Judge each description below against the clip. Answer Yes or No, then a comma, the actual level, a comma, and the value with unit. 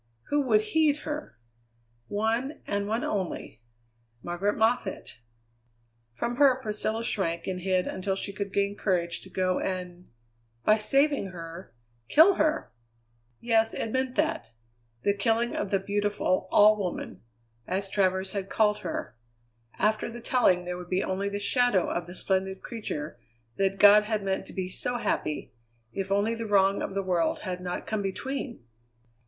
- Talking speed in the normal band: Yes, average, 160 wpm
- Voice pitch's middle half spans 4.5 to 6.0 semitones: No, average, 3.2 semitones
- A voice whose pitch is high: Yes, high, 200 Hz